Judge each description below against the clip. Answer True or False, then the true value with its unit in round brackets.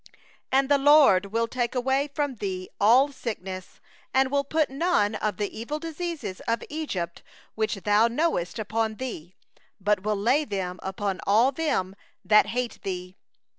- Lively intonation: True (5.8 semitones)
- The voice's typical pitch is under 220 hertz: False (225 Hz)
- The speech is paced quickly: False (160 wpm)